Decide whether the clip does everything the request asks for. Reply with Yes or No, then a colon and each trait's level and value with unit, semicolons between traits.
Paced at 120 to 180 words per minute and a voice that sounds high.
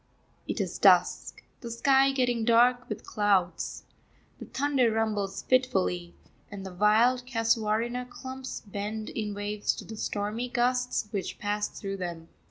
Yes: average, 140 wpm; high, 220 Hz